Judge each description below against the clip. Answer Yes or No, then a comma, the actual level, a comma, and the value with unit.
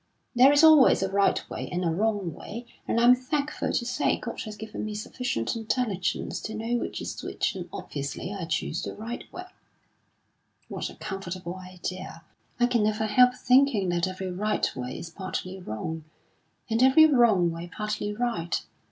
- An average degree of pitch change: Yes, average, 5.0 semitones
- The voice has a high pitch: Yes, high, 210 Hz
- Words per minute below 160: No, average, 175 wpm